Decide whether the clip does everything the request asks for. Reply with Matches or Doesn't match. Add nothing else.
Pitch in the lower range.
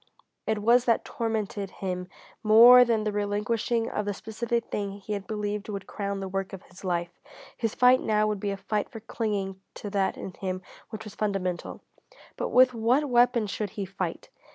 Doesn't match